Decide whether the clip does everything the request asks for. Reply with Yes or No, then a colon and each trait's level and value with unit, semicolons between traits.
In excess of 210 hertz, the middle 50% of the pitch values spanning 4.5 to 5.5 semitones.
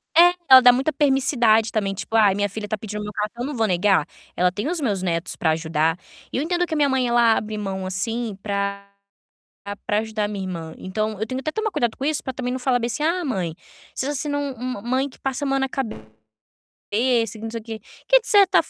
Yes: high, 225 Hz; average, 4.8 semitones